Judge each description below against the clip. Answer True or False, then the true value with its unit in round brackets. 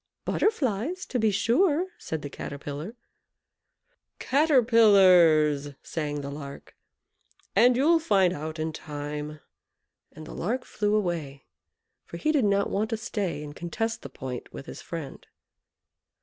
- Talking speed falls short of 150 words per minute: True (135 wpm)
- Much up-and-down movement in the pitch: True (7.4 semitones)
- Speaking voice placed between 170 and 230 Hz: True (185 Hz)